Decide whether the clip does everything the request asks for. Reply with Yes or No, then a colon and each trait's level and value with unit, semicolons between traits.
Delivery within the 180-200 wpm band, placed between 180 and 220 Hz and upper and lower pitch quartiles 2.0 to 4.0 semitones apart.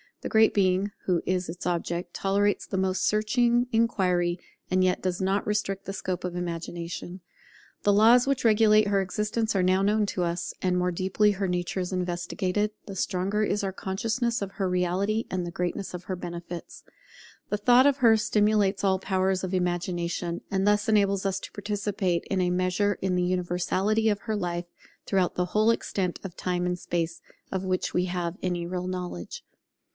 Yes: average, 190 wpm; high, 190 Hz; narrow, 2.5 semitones